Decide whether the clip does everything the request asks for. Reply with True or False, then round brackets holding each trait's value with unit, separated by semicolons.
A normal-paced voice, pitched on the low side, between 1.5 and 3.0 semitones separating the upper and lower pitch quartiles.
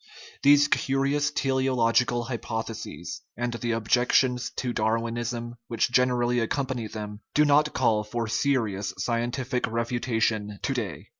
False (130 wpm; 120 Hz; 2.5 semitones)